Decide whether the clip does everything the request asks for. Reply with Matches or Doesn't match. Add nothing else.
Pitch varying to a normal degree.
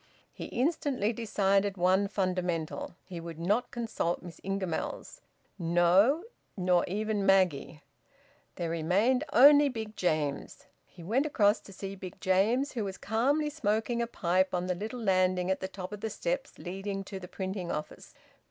Matches